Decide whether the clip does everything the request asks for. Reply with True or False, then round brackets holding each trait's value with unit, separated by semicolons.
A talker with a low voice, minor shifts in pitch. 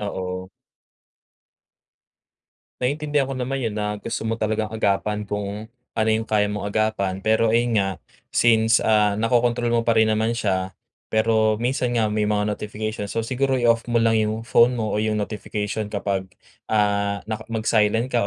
True (110 Hz; 1.8 semitones)